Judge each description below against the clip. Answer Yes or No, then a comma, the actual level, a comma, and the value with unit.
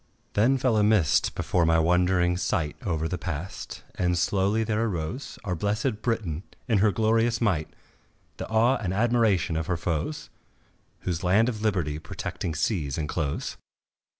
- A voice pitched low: Yes, very low, 95 Hz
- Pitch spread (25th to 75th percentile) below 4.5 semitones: No, average, 5.1 semitones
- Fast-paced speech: No, average, 150 wpm